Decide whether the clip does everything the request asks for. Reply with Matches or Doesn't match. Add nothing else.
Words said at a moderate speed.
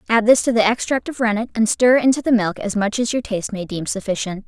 Doesn't match